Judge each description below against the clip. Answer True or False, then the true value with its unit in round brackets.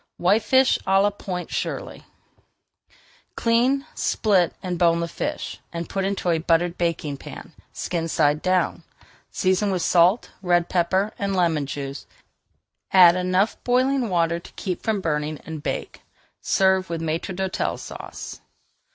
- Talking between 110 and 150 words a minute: True (140 wpm)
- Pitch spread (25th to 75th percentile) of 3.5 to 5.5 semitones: False (2.7 semitones)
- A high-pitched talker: False (180 Hz)